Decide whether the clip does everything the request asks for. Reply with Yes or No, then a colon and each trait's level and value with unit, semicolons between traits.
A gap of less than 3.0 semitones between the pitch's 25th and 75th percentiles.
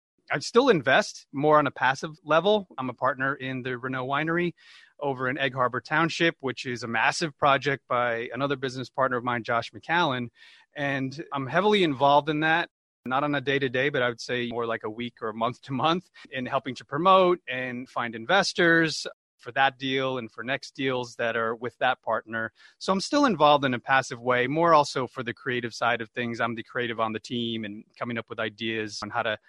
No: average, 3.3 semitones